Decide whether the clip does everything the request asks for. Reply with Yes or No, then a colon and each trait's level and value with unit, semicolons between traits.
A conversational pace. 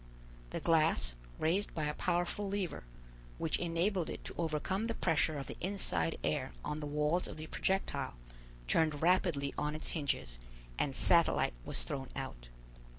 Yes: average, 155 wpm